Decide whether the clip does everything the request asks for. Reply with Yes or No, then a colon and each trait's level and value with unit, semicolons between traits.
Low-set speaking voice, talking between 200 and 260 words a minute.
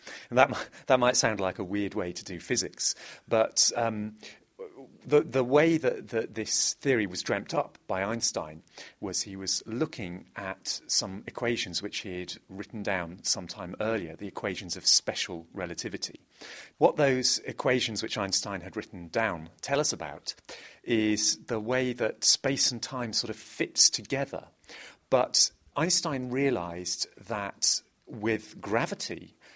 No: low, 110 Hz; average, 150 wpm